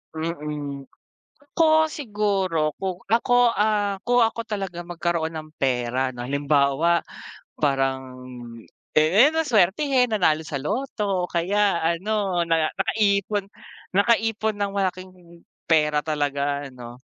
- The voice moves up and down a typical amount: No, wide, 6.0 semitones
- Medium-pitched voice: Yes, medium, 175 Hz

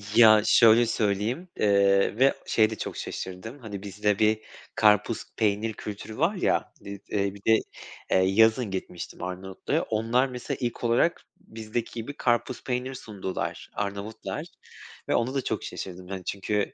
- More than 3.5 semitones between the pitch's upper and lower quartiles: No, average, 3.0 semitones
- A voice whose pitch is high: No, low, 110 Hz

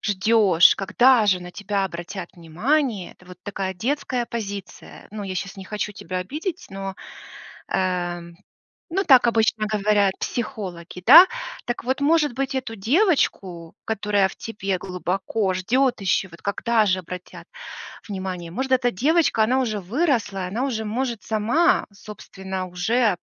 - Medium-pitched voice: No, high, 210 Hz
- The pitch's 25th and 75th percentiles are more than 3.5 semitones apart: Yes, average, 4.7 semitones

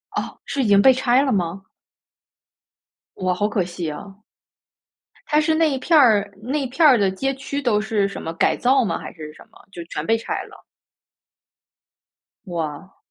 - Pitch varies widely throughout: Yes, wide, 6.5 semitones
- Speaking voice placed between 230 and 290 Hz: No, high, 210 Hz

